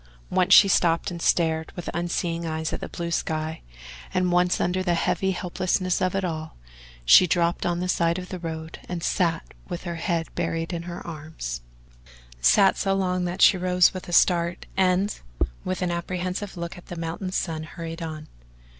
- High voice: No, medium, 175 Hz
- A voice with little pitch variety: Yes, narrow, 1.8 semitones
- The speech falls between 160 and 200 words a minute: Yes, average, 185 wpm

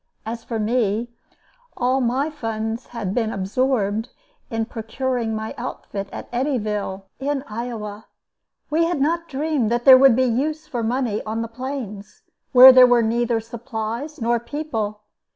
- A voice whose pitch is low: No, high, 235 Hz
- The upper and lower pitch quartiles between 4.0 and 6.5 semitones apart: No, average, 3.1 semitones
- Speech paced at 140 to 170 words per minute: Yes, average, 150 wpm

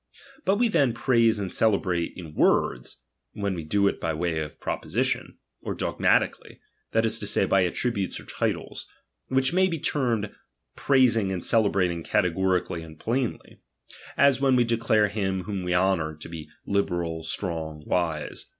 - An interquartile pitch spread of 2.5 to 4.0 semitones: No, wide, 5.4 semitones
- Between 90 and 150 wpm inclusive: No, average, 165 wpm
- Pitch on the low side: Yes, low, 100 Hz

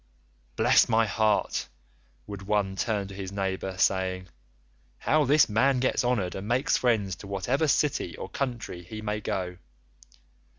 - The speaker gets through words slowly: No, average, 145 wpm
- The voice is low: Yes, low, 105 Hz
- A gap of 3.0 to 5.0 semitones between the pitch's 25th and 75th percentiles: Yes, average, 4.3 semitones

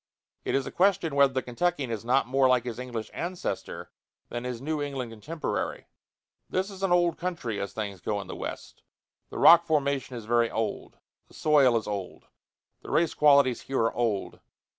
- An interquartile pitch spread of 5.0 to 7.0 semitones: Yes, wide, 5.4 semitones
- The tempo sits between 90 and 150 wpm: No, average, 185 wpm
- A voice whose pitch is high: No, low, 130 Hz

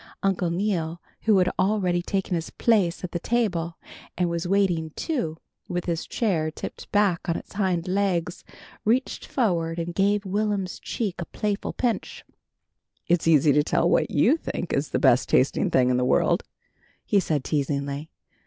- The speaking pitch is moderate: Yes, medium, 175 Hz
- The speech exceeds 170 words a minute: No, average, 165 wpm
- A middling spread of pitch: Yes, average, 3.5 semitones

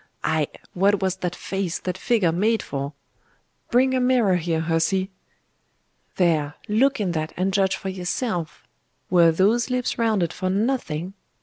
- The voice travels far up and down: No, average, 4.4 semitones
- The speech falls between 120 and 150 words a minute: Yes, average, 145 wpm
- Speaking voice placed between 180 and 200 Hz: Yes, high, 190 Hz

